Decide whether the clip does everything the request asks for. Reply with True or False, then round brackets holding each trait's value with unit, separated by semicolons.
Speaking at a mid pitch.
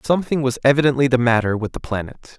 False (130 Hz)